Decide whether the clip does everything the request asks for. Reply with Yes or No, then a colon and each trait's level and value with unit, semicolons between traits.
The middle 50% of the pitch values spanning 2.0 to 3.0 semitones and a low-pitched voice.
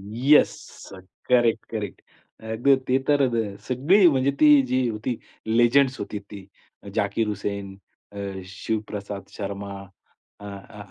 No: average, 4.3 semitones; low, 110 Hz